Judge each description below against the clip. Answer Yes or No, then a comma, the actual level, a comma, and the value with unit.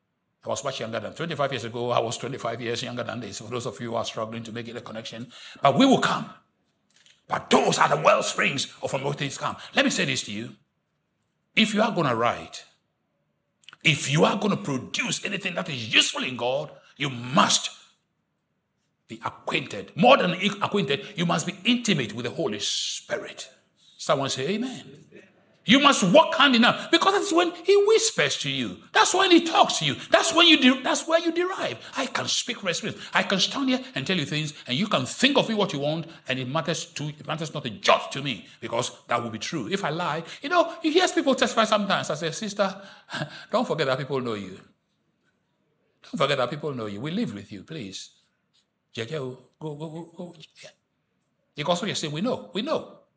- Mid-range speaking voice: Yes, medium, 165 Hz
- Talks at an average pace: No, fast, 210 wpm